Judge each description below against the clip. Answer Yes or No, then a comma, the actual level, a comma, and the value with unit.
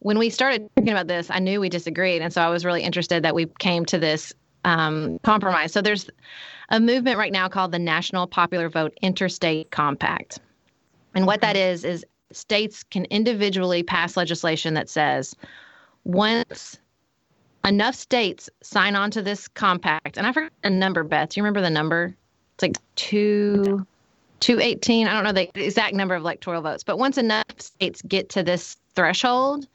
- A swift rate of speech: No, average, 180 wpm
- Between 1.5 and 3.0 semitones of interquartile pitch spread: No, average, 3.5 semitones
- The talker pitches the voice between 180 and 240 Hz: Yes, medium, 185 Hz